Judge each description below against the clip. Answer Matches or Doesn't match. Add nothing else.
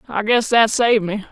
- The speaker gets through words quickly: Matches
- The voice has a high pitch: Matches